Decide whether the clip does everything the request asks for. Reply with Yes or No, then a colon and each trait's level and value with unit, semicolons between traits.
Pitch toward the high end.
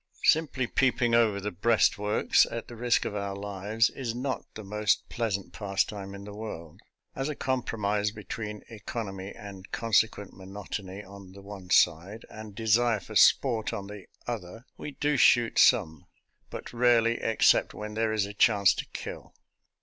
No: low, 105 Hz